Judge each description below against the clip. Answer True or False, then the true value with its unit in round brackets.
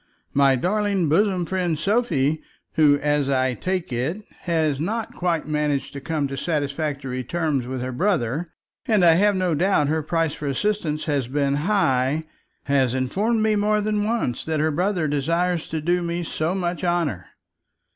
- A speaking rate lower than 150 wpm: False (165 wpm)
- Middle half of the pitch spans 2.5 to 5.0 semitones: True (4.7 semitones)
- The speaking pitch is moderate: True (160 Hz)